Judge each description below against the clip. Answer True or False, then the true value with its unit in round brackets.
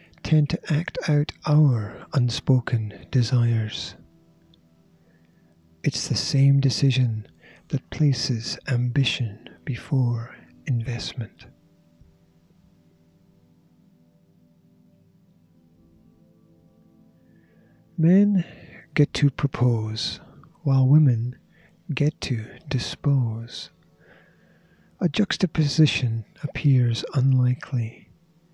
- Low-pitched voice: True (130 Hz)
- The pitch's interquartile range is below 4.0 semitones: False (5.0 semitones)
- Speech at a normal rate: False (60 wpm)